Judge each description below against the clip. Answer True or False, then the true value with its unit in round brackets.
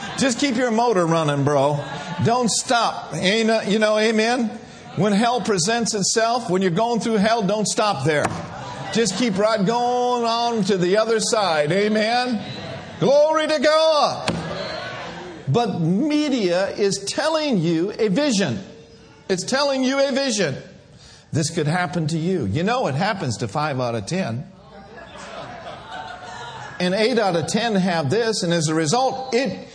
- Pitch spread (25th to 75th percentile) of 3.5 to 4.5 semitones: False (5.4 semitones)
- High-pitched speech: True (215 Hz)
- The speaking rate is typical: True (150 wpm)